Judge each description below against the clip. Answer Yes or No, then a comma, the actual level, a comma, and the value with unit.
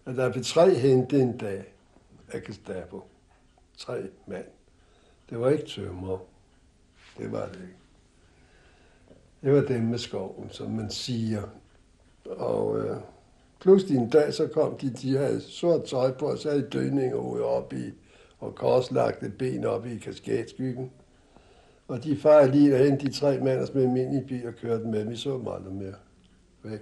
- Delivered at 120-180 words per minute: Yes, average, 170 wpm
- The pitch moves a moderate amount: No, wide, 6.3 semitones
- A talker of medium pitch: No, low, 125 Hz